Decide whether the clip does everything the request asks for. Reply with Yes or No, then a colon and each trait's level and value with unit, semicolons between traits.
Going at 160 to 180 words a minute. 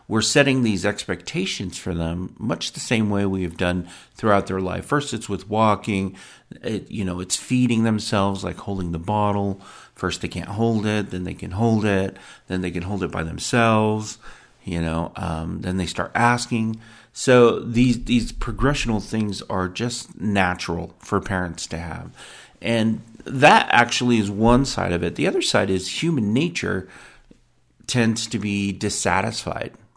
Yes: average, 170 wpm